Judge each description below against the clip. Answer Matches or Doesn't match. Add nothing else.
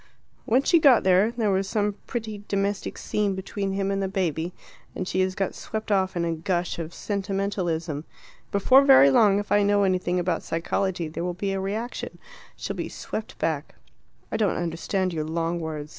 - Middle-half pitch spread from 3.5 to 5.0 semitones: Doesn't match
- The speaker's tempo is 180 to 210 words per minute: Matches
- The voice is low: Doesn't match